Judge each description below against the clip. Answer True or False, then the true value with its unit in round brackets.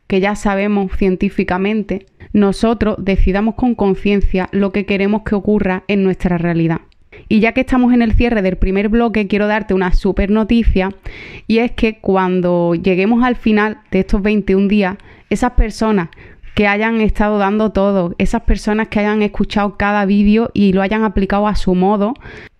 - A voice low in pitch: False (205 Hz)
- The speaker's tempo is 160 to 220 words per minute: True (165 wpm)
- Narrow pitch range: True (2.0 semitones)